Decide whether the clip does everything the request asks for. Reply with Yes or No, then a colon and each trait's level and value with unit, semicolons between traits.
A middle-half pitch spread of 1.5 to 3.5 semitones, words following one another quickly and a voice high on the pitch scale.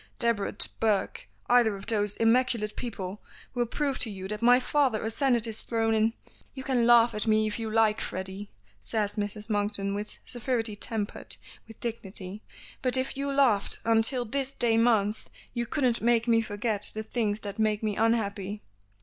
No: narrow, 2.5 semitones; average, 175 wpm; high, 225 Hz